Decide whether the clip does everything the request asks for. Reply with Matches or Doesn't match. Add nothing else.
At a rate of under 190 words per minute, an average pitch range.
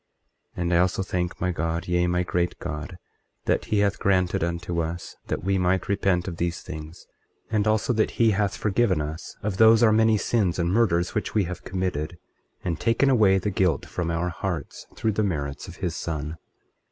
Doesn't match